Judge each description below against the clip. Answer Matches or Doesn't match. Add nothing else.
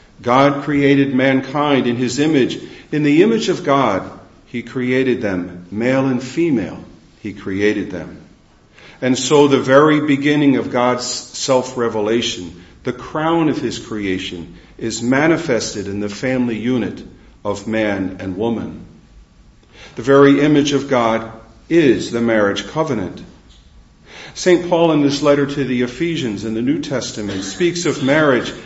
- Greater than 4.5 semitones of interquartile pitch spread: Matches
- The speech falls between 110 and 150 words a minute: Matches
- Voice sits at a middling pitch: Doesn't match